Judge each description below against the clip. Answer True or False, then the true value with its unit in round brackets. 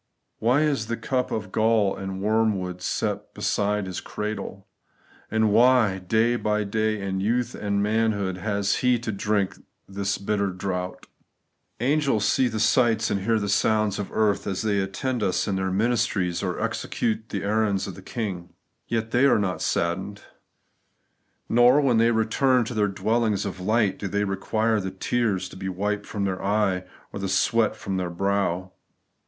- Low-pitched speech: True (105 Hz)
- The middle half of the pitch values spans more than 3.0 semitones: False (2.6 semitones)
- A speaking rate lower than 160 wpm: False (170 wpm)